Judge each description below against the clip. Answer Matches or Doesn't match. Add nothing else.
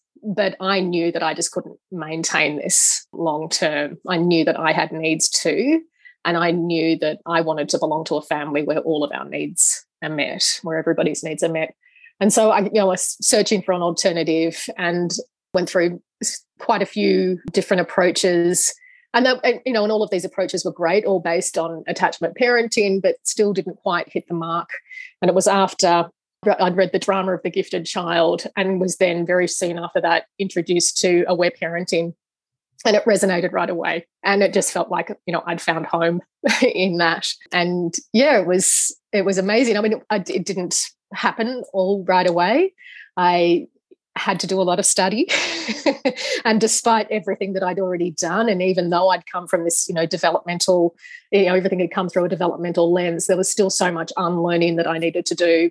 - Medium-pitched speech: Matches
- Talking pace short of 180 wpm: Doesn't match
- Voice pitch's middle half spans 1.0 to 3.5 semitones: Matches